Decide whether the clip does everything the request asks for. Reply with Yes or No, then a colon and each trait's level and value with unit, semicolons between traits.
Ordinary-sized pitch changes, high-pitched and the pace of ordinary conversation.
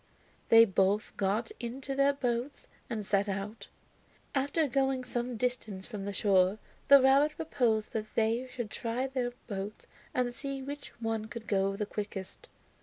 Yes: average, 4.1 semitones; high, 230 Hz; average, 155 wpm